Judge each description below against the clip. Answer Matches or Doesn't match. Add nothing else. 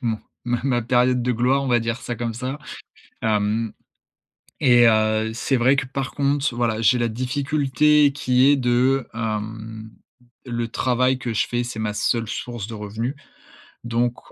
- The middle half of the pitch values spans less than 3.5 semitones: Matches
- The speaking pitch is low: Matches